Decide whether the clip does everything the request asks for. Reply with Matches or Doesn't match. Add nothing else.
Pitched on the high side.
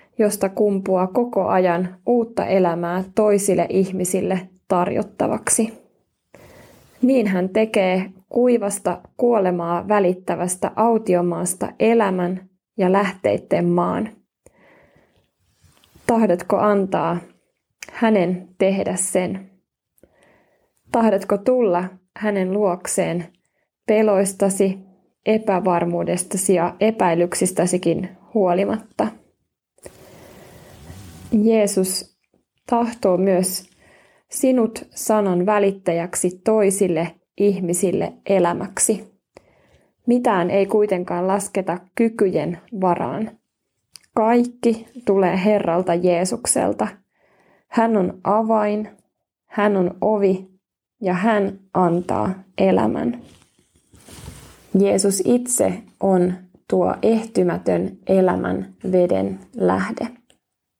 Matches